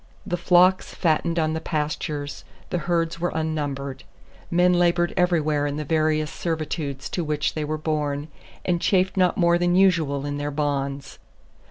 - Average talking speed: Yes, average, 160 wpm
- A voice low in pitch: No, medium, 155 Hz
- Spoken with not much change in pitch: No, average, 3.0 semitones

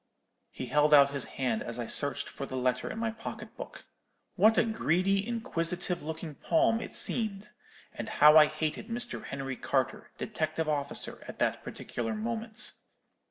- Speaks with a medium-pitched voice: Yes, medium, 165 Hz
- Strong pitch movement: Yes, wide, 7.6 semitones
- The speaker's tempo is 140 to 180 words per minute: Yes, average, 160 wpm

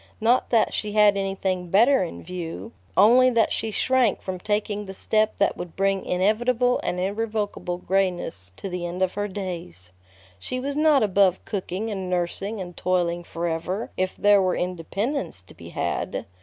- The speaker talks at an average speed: Yes, average, 170 wpm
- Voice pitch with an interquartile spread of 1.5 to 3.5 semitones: Yes, average, 3.2 semitones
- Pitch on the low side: No, high, 195 Hz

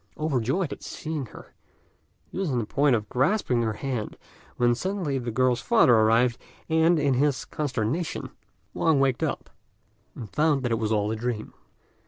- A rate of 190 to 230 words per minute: No, average, 170 wpm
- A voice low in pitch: Yes, low, 130 Hz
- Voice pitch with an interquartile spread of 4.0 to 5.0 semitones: Yes, average, 4.6 semitones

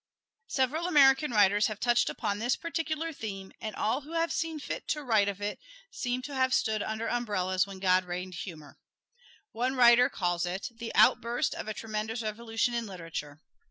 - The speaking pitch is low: No, high, 225 Hz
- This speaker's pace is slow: No, average, 180 wpm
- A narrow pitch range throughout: No, average, 4.8 semitones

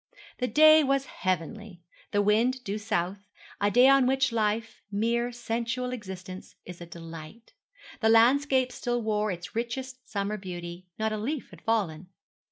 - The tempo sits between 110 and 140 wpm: No, average, 155 wpm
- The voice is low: No, high, 220 Hz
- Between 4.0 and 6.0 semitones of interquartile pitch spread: Yes, average, 4.7 semitones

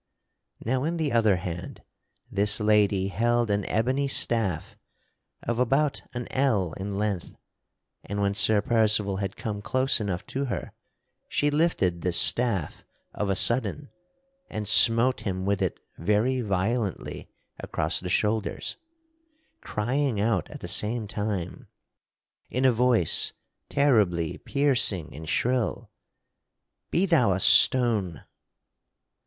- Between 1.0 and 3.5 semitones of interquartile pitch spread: No, average, 4.3 semitones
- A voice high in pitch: No, low, 110 Hz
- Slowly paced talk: Yes, slow, 125 wpm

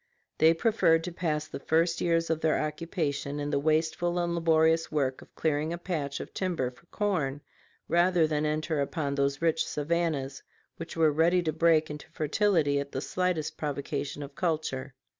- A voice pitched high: No, medium, 160 Hz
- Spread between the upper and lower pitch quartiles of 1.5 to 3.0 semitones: Yes, narrow, 2.6 semitones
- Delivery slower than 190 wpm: Yes, average, 175 wpm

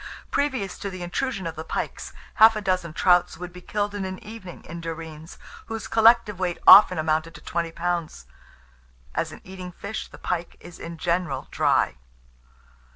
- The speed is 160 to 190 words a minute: Yes, average, 170 wpm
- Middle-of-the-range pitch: Yes, medium, 180 Hz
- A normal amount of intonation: Yes, average, 3.5 semitones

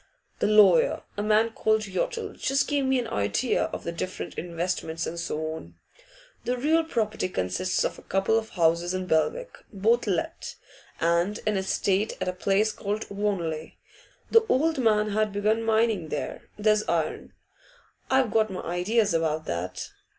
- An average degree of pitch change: Yes, average, 4.6 semitones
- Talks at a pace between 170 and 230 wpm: No, average, 160 wpm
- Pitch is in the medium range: No, high, 205 Hz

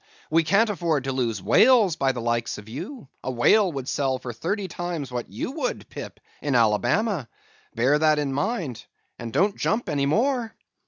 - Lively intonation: Yes, wide, 8.4 semitones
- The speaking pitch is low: No, medium, 145 Hz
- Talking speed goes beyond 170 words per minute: Yes, average, 180 wpm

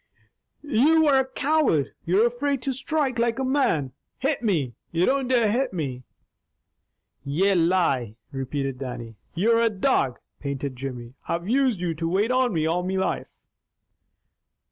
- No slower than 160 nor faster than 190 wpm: No, average, 150 wpm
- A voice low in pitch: No, high, 190 Hz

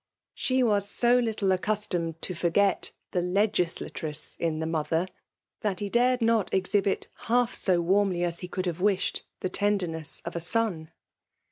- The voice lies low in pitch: No, high, 190 Hz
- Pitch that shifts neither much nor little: Yes, average, 3.6 semitones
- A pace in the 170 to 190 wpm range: No, average, 155 wpm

